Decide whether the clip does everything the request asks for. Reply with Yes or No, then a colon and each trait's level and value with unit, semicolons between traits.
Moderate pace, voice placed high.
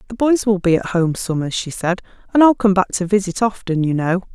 No: fast, 235 wpm; high, 195 Hz